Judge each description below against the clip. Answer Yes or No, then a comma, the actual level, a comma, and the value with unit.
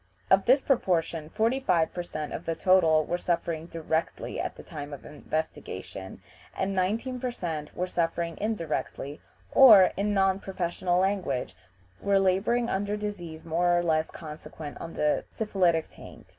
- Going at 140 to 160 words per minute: Yes, average, 150 wpm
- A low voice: No, medium, 175 Hz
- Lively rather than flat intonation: No, average, 3.7 semitones